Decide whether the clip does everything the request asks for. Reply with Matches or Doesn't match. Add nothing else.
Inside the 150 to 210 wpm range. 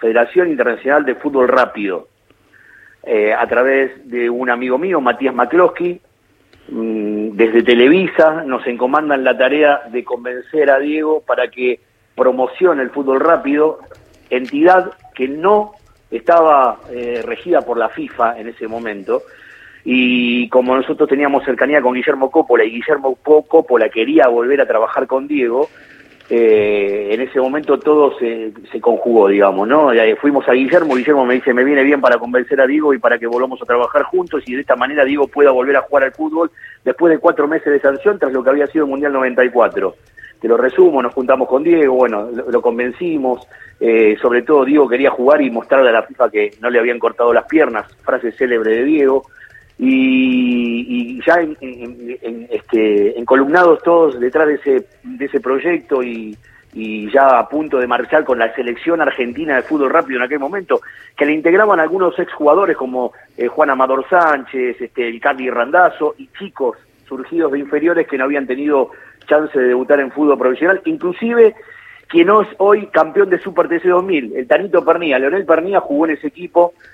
Matches